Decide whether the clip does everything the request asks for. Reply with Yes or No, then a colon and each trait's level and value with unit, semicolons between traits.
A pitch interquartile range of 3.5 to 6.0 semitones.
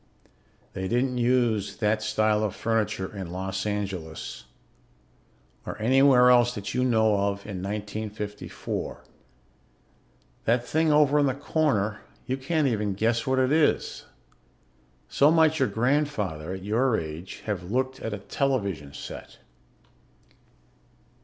Yes: average, 4.7 semitones